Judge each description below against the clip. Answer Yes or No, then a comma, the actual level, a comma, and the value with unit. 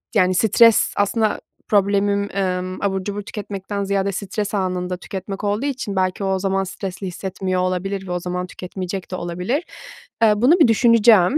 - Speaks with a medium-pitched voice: No, high, 195 Hz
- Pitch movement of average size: No, narrow, 2.0 semitones